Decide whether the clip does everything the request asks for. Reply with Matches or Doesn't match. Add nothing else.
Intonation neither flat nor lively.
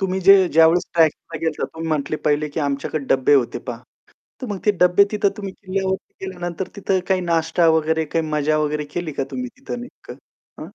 Matches